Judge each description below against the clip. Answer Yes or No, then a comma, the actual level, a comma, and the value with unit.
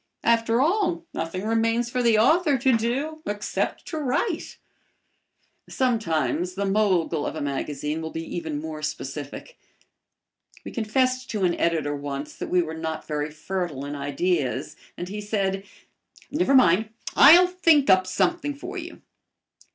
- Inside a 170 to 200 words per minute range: No, average, 145 wpm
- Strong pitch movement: Yes, wide, 8.5 semitones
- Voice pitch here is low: No, high, 200 Hz